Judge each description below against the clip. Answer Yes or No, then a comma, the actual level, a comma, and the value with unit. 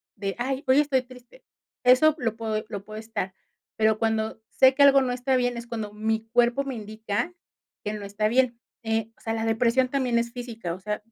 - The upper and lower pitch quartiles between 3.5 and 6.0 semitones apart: No, average, 2.7 semitones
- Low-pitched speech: No, high, 230 Hz